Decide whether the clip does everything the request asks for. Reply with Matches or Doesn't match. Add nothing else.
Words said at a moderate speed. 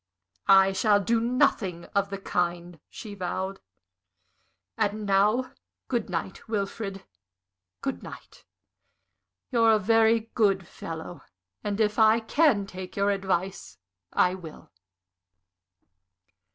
Doesn't match